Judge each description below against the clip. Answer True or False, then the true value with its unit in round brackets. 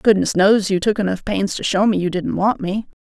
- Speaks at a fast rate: True (255 wpm)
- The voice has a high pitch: True (200 Hz)